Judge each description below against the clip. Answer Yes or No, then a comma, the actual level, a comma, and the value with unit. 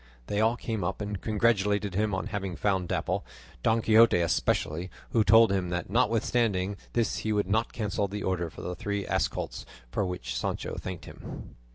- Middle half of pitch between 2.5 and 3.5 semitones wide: Yes, average, 3.0 semitones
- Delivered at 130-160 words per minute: No, average, 185 wpm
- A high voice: No, low, 100 Hz